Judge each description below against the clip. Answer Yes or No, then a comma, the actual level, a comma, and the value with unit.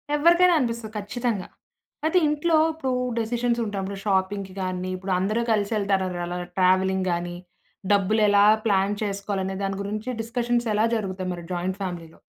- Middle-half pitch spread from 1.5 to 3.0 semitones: No, average, 3.6 semitones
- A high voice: Yes, high, 200 Hz